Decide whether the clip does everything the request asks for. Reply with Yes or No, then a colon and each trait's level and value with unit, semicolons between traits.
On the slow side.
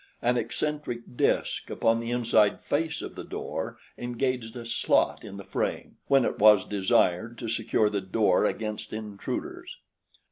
No: average, 150 wpm